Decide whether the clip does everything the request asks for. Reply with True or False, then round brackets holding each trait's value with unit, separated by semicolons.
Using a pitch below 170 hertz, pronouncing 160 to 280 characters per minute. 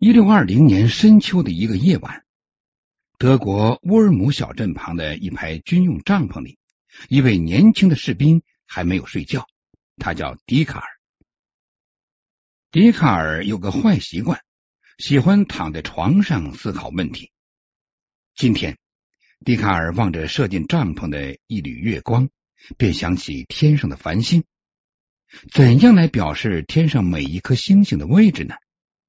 True (135 Hz; 210 characters per minute)